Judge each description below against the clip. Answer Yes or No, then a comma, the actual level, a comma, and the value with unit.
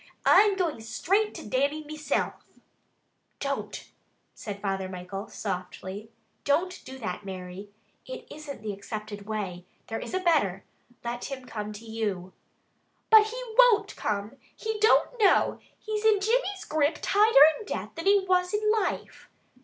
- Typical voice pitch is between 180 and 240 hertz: No, very high, 280 Hz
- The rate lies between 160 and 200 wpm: No, average, 145 wpm